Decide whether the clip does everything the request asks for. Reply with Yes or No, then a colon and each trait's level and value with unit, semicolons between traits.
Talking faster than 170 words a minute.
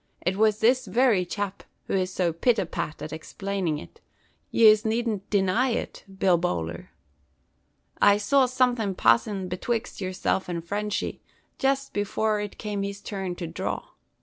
No: average, 150 wpm